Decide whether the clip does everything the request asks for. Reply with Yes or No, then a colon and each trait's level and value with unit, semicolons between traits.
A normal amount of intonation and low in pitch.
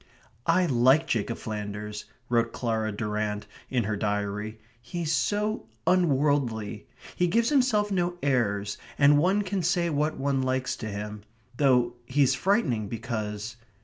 No: wide, 7.7 semitones; low, 125 Hz